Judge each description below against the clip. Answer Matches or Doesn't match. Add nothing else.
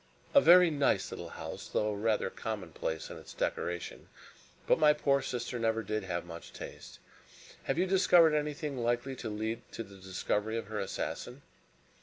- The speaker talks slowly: Doesn't match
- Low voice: Matches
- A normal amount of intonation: Doesn't match